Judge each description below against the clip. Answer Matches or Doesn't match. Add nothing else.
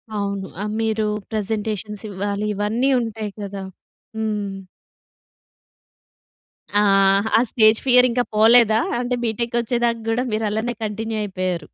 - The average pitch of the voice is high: Matches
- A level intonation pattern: Matches